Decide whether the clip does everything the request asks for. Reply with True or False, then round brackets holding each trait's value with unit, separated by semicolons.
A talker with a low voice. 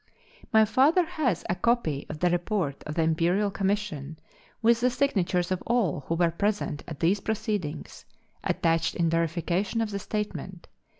False (185 Hz)